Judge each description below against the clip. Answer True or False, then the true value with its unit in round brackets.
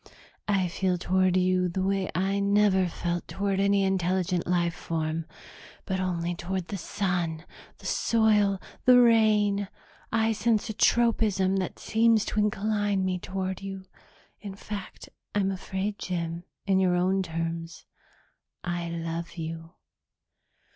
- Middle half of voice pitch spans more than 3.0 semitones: False (2.5 semitones)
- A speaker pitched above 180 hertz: True (190 Hz)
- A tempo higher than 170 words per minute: False (135 wpm)